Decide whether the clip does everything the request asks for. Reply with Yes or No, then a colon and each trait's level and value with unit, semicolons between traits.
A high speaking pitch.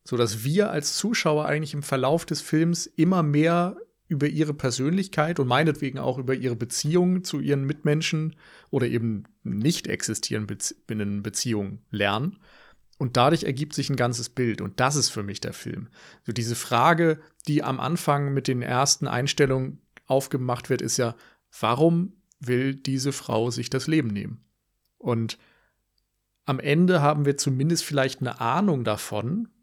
No: medium, 140 Hz